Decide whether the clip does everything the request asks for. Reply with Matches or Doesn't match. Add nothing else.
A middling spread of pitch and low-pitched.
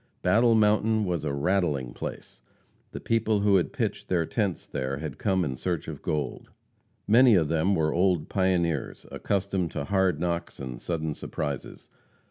Matches